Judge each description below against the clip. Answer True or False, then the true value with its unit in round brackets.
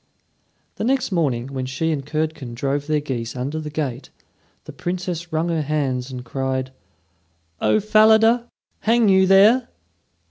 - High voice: False (155 Hz)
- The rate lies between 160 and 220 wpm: False (145 wpm)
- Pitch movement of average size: False (6.3 semitones)